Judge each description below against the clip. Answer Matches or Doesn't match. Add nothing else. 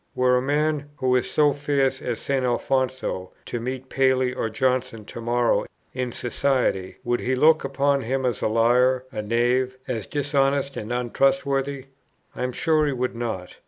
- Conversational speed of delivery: Matches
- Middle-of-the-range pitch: Doesn't match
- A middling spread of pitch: Doesn't match